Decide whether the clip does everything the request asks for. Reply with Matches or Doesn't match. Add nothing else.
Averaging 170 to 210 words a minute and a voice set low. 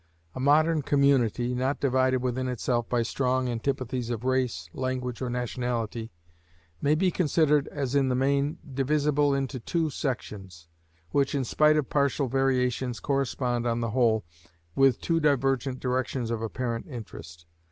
Doesn't match